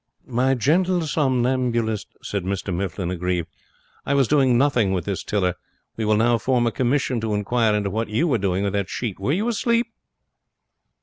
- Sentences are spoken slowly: No, average, 180 wpm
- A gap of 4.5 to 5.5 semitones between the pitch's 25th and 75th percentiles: Yes, average, 5.0 semitones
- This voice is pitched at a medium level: No, low, 115 Hz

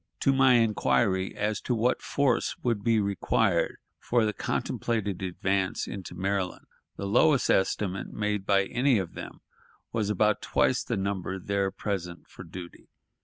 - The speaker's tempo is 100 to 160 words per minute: Yes, average, 150 wpm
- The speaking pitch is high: No, low, 100 Hz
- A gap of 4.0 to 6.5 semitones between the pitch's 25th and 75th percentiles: No, average, 3.2 semitones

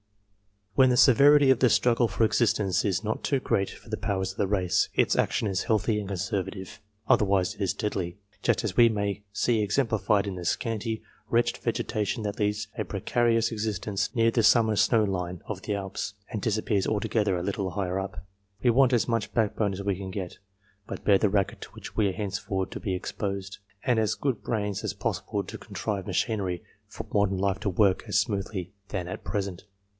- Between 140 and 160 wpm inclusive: No, average, 200 wpm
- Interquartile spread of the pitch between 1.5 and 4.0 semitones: Yes, narrow, 2.6 semitones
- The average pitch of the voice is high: No, low, 105 Hz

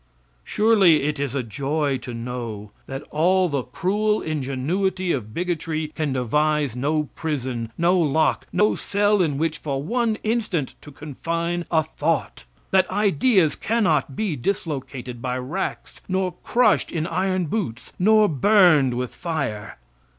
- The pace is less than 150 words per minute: Yes, average, 140 wpm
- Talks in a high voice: No, medium, 155 Hz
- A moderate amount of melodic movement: No, wide, 5.7 semitones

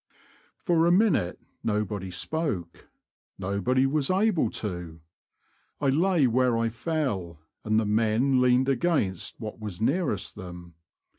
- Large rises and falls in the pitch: Yes, wide, 6.8 semitones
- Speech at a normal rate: No, slow, 130 wpm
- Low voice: Yes, low, 115 Hz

